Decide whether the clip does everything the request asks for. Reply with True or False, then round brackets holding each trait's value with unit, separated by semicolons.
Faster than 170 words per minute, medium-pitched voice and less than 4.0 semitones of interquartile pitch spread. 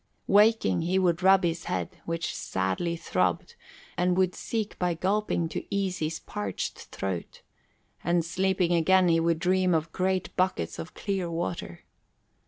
False (150 wpm; 175 Hz; 2.5 semitones)